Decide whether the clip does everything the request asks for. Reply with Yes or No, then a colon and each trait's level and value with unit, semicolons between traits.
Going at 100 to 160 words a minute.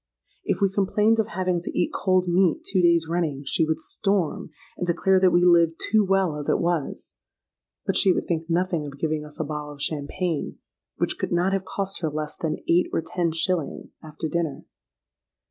No: average, 195 wpm